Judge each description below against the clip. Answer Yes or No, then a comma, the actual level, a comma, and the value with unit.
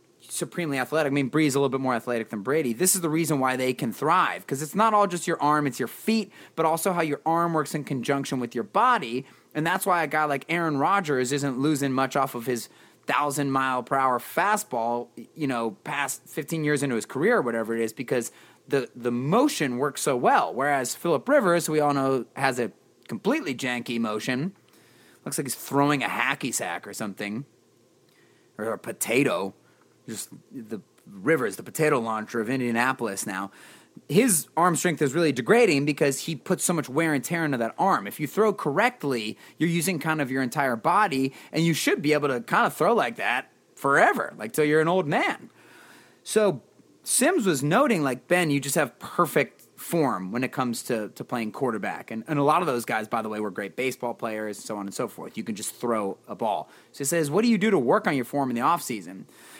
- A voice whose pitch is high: No, medium, 140 Hz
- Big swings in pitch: No, average, 4.8 semitones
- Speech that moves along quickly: Yes, fast, 220 wpm